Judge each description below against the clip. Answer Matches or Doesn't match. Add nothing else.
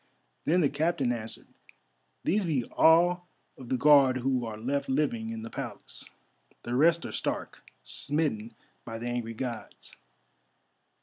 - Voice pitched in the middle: Doesn't match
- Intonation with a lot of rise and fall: Doesn't match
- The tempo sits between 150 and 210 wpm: Doesn't match